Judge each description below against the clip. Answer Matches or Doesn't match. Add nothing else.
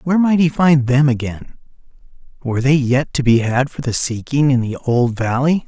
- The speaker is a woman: Doesn't match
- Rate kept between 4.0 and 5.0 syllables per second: Doesn't match